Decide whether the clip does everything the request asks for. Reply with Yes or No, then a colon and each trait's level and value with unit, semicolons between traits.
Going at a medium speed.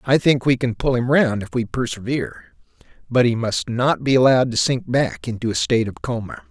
No: fast, 220 wpm